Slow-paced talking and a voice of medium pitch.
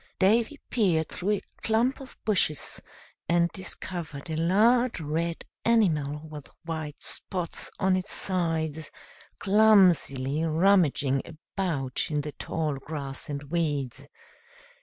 Yes: slow, 115 wpm; medium, 165 Hz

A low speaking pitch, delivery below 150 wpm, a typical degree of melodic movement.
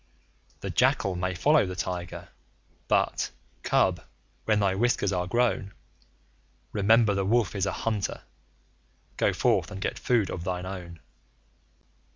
Yes: very low, 95 Hz; slow, 135 wpm; average, 3.0 semitones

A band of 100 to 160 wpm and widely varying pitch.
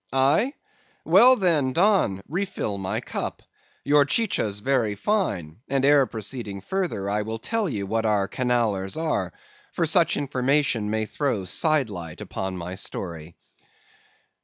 Yes: slow, 135 wpm; wide, 7.6 semitones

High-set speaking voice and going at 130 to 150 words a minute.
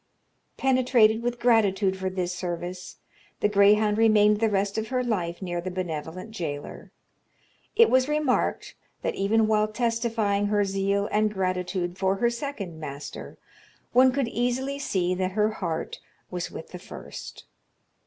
Yes: high, 205 Hz; average, 145 wpm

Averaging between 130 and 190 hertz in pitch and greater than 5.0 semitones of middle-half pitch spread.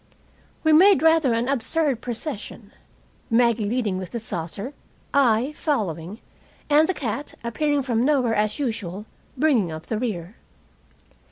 No: high, 235 Hz; wide, 5.4 semitones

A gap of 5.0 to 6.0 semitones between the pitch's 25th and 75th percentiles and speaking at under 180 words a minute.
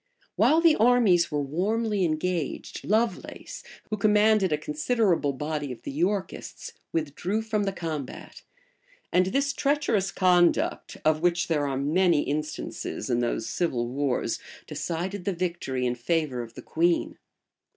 Yes: wide, 5.6 semitones; average, 140 wpm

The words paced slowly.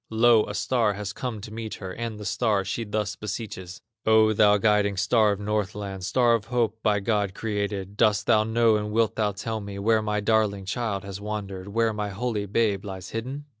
No: fast, 205 wpm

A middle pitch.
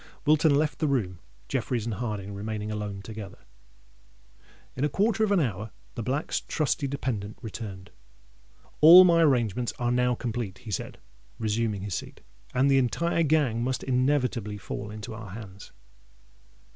No: low, 120 Hz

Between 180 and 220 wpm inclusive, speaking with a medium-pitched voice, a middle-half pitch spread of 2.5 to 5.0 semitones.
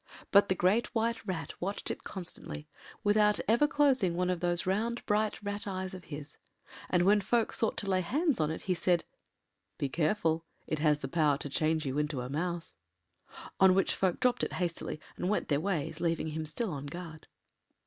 Yes: average, 195 wpm; medium, 180 Hz; average, 4.6 semitones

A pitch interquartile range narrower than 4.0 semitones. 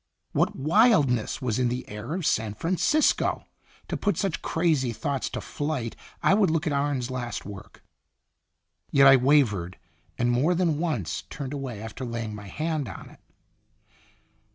No: average, 5.3 semitones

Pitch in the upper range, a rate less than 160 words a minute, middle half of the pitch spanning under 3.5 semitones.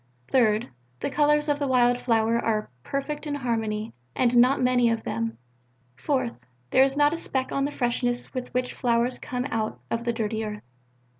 No: high, 245 Hz; average, 180 wpm; average, 3.0 semitones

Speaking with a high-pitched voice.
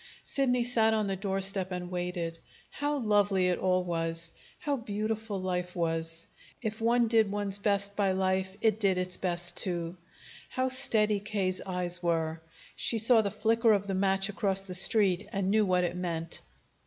Yes: high, 195 Hz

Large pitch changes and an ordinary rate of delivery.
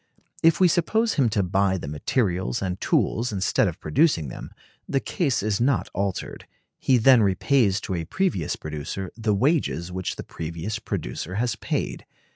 Yes: wide, 6.1 semitones; average, 165 wpm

